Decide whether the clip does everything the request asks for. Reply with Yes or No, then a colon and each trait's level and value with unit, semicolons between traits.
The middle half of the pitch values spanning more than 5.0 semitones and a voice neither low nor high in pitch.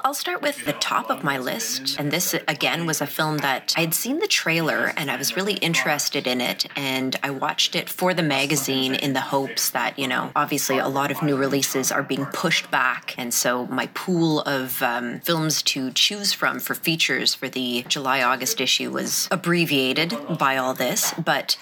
No: average, 3.7 semitones; medium, 145 Hz